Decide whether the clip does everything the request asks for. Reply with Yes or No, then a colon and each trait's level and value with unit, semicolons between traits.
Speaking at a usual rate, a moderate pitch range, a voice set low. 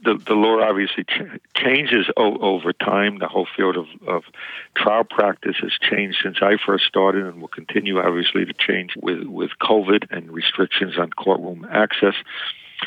No: average, 170 wpm; narrow, 2.3 semitones; low, 100 Hz